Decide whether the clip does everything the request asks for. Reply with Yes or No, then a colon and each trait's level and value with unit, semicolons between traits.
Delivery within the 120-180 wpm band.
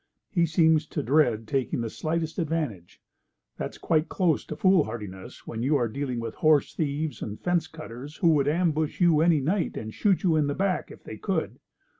No: average, 190 wpm